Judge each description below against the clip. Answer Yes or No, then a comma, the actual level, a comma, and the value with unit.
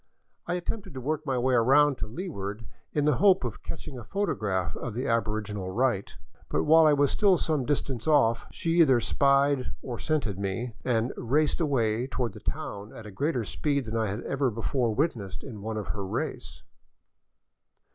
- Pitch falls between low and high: No, low, 125 Hz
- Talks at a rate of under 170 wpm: No, average, 185 wpm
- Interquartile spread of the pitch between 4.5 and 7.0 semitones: Yes, average, 5.2 semitones